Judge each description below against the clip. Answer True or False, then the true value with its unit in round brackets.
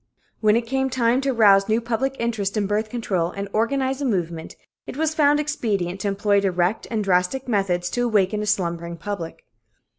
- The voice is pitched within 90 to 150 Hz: False (210 Hz)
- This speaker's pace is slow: False (185 wpm)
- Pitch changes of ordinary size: True (4.1 semitones)